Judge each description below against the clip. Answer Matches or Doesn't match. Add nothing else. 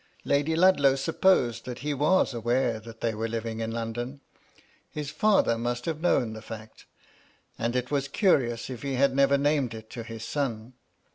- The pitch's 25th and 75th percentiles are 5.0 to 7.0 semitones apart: Doesn't match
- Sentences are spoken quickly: Doesn't match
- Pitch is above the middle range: Doesn't match